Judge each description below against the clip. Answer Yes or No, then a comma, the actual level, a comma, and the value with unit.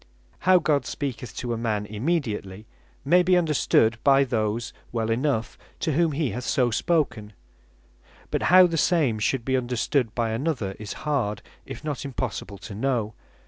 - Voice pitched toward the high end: No, low, 125 Hz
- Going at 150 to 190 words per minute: Yes, average, 160 wpm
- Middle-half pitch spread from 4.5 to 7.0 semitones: Yes, average, 5.3 semitones